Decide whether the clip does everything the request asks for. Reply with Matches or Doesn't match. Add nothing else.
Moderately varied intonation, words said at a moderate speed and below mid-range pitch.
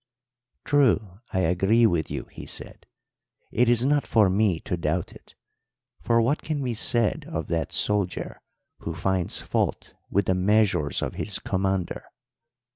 Matches